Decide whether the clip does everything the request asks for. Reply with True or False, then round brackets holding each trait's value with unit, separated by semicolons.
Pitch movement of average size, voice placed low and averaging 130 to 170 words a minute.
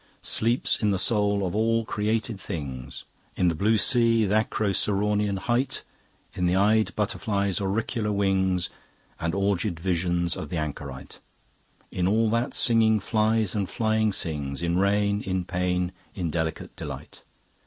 True (3.5 semitones; 100 Hz; 145 wpm)